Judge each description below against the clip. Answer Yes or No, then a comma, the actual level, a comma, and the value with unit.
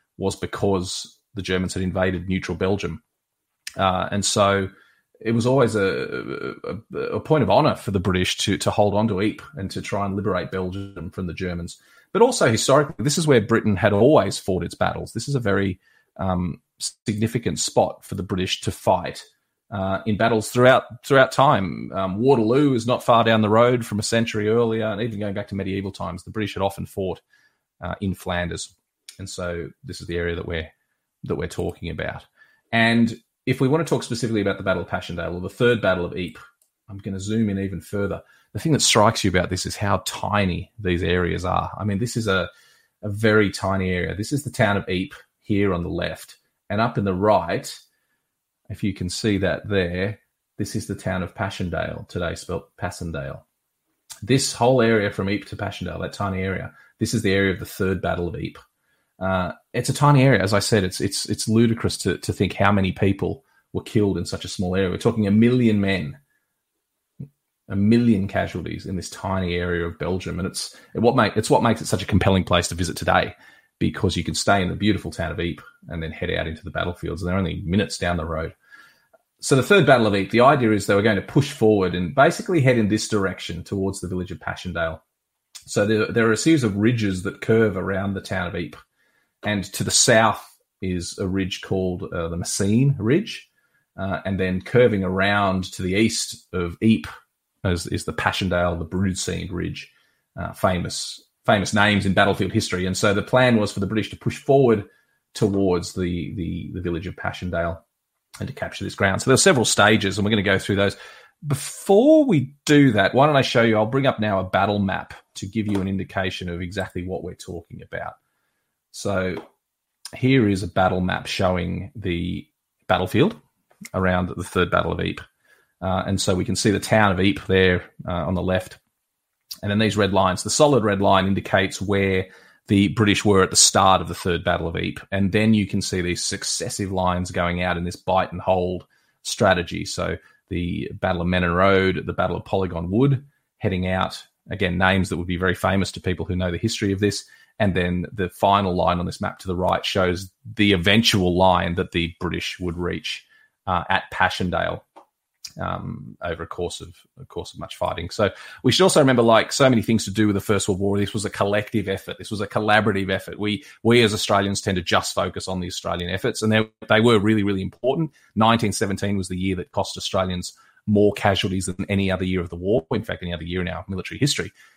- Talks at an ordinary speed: No, fast, 215 wpm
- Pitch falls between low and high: No, very low, 95 Hz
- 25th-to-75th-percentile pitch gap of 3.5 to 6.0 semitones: No, average, 2.9 semitones